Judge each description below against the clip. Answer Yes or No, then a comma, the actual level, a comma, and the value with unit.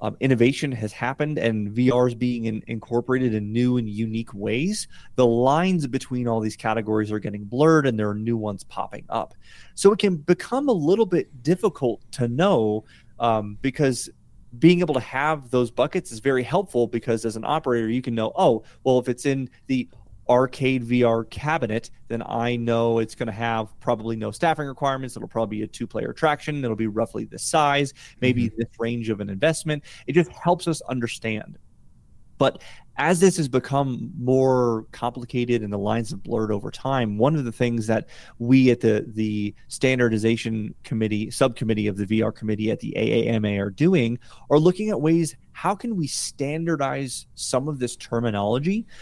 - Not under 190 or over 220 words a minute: No, average, 180 wpm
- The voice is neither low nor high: No, low, 120 Hz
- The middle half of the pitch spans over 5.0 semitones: No, average, 3.7 semitones